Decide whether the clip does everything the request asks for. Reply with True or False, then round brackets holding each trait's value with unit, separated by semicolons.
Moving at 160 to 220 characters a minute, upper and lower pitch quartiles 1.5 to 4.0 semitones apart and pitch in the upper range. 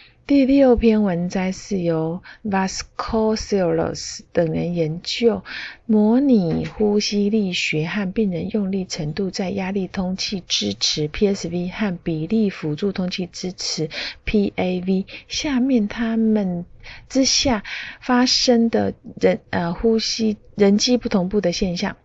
True (210 characters per minute; 3.7 semitones; 200 Hz)